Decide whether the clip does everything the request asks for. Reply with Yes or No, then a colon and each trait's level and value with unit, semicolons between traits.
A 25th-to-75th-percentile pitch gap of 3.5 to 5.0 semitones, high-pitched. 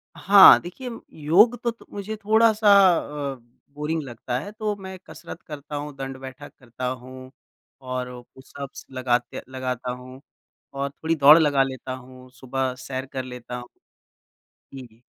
No: average, 4.2 semitones; low, 135 Hz